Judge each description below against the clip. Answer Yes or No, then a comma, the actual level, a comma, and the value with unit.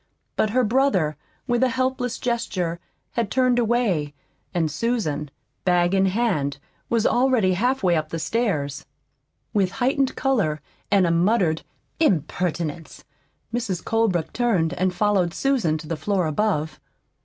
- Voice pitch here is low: No, high, 195 Hz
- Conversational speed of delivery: No, slow, 130 wpm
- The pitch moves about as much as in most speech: No, wide, 6.5 semitones